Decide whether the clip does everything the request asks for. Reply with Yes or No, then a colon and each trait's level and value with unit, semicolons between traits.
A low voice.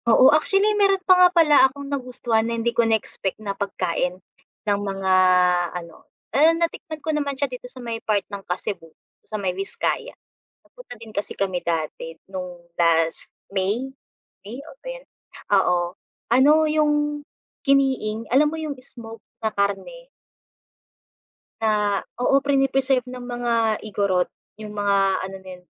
No: high, 230 Hz